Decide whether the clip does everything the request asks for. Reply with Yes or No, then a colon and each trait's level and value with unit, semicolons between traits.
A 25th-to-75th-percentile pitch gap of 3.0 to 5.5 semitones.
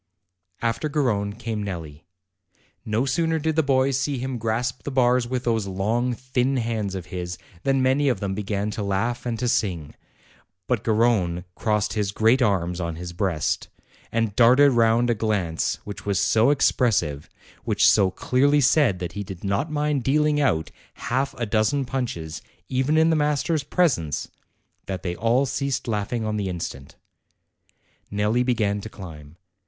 Yes: average, 5.0 semitones